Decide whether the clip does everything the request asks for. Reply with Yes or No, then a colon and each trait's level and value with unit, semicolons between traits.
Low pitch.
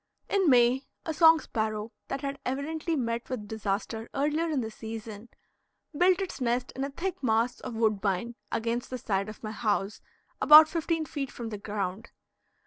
No: high, 240 Hz